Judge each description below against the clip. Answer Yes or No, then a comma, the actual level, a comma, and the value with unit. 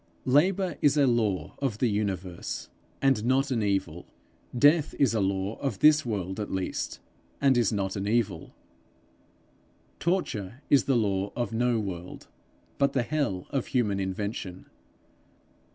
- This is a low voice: Yes, low, 115 Hz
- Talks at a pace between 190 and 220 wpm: No, average, 150 wpm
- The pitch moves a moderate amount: No, wide, 5.8 semitones